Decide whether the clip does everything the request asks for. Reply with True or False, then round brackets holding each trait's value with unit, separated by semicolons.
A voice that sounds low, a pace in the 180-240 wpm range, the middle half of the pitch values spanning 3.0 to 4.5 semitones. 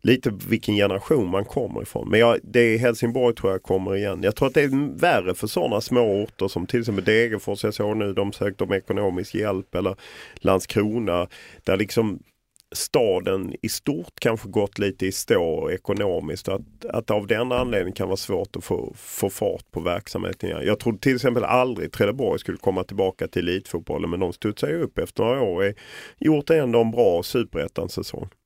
True (110 Hz; 185 wpm; 3.6 semitones)